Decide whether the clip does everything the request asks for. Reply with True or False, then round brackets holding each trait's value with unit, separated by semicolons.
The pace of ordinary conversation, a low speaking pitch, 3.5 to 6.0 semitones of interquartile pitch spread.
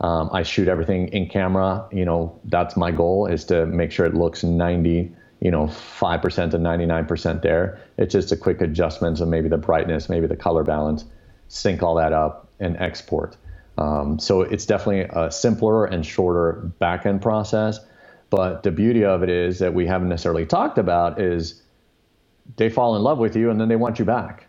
False (195 wpm; 85 Hz; 3.1 semitones)